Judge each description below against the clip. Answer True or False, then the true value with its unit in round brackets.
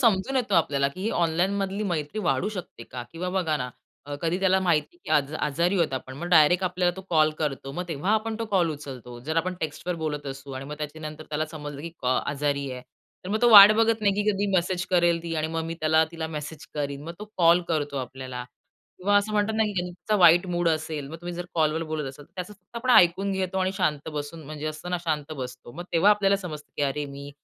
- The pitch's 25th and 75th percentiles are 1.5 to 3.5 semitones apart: False (4.2 semitones)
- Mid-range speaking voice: True (165 Hz)